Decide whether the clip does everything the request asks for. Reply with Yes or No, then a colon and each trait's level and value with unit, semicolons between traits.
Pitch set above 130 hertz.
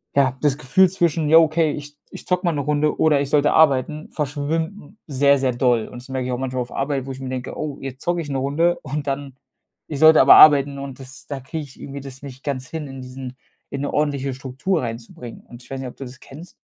Yes: medium, 140 Hz